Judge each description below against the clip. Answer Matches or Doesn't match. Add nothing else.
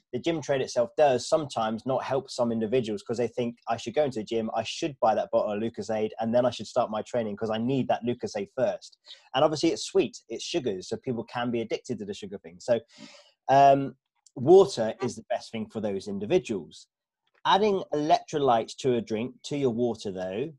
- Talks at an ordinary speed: Doesn't match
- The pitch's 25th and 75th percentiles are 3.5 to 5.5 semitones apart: Matches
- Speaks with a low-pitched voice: Matches